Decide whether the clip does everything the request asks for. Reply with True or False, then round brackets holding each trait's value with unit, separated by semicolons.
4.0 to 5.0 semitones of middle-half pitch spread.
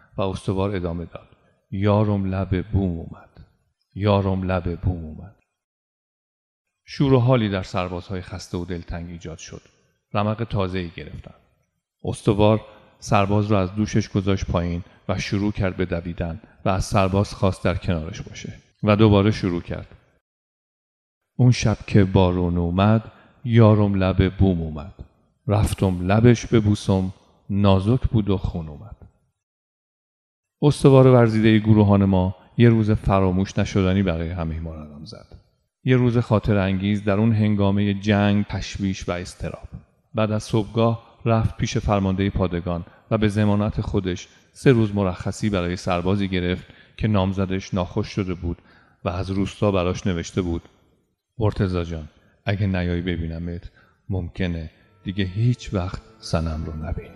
False (2.9 semitones)